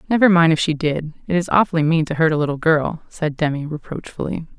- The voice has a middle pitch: Yes, medium, 160 Hz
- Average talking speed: No, fast, 220 wpm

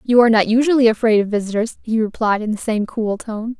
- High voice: Yes, high, 225 Hz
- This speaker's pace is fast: Yes, fast, 235 wpm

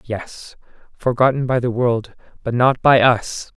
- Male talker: Yes, male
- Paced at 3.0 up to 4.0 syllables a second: Yes, 3.9 syllables/s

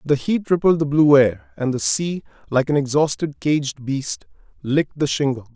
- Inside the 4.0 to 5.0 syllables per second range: Yes, 4.6 syllables/s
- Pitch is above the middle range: No, medium, 145 Hz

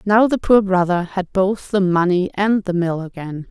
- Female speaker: Yes, female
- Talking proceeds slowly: No, fast, 205 wpm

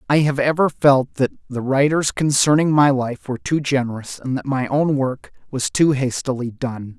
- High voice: No, low, 135 Hz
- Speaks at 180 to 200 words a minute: Yes, average, 190 wpm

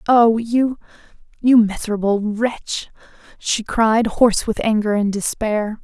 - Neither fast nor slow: No, slow, 115 wpm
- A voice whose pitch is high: Yes, high, 220 Hz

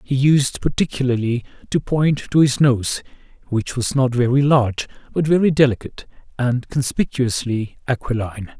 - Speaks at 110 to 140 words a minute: Yes, slow, 135 wpm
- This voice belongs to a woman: No, male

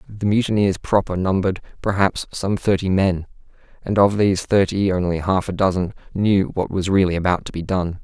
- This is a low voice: Yes, very low, 95 Hz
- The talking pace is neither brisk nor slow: Yes, average, 180 wpm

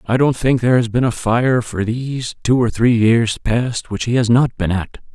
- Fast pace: Yes, fast, 245 wpm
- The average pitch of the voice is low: Yes, low, 120 Hz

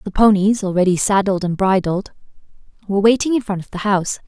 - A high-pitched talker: Yes, high, 200 Hz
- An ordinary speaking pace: Yes, average, 180 wpm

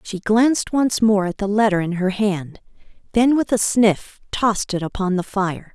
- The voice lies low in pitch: No, high, 205 Hz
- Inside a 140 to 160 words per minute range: No, average, 200 wpm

